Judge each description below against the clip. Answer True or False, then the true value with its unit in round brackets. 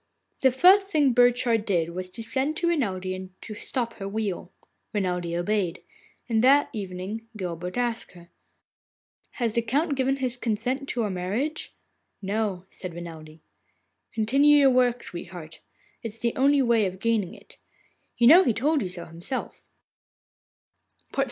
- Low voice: False (225 Hz)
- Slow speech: False (150 wpm)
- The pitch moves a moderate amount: False (5.9 semitones)